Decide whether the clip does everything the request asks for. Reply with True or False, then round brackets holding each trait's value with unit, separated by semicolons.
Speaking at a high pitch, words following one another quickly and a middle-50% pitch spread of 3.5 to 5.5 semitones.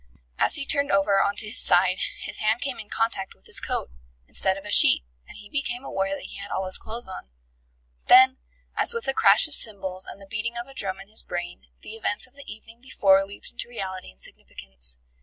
True (205 Hz; 230 wpm; 3.9 semitones)